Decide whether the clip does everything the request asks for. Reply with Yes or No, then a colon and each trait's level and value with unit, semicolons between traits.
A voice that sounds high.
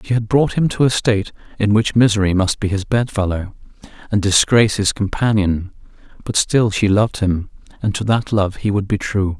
No: low, 105 Hz